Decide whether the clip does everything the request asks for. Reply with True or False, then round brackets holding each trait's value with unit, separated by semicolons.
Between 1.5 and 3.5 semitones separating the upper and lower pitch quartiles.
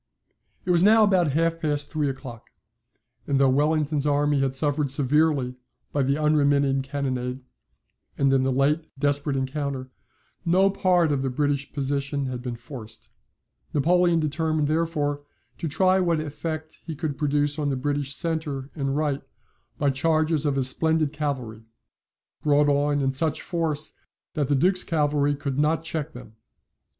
True (2.4 semitones)